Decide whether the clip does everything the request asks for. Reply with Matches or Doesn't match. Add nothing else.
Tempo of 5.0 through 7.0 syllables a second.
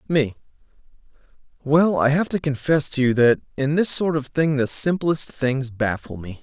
Doesn't match